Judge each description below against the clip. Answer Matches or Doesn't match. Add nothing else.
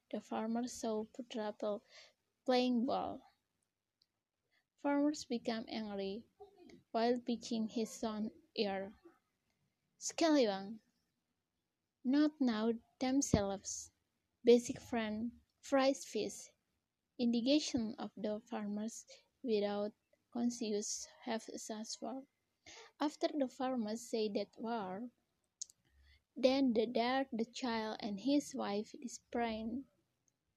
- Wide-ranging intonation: Doesn't match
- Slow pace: Matches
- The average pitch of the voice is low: Doesn't match